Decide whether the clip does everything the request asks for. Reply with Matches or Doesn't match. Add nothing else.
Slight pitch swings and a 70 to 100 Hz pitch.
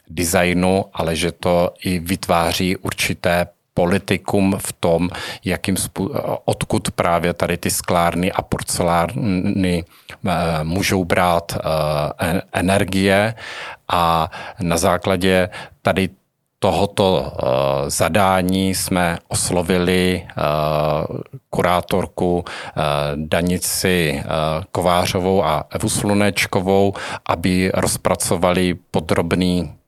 Matches